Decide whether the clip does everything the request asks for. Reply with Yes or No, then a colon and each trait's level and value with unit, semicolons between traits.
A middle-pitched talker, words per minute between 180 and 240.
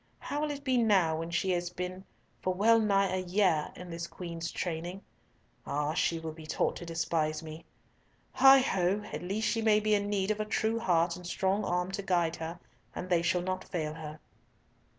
Yes: medium, 180 Hz; fast, 205 wpm